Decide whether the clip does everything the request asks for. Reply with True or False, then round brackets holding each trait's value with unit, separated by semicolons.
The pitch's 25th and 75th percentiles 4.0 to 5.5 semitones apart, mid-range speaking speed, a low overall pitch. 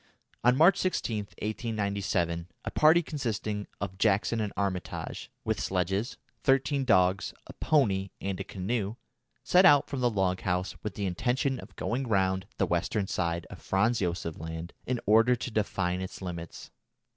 True (4.7 semitones; 155 wpm; 100 Hz)